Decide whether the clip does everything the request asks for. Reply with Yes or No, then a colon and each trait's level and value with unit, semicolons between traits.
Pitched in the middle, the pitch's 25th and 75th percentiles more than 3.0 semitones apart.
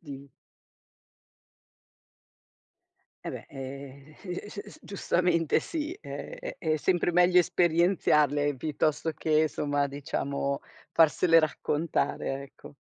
Yes: medium, 155 Hz; average, 3.5 semitones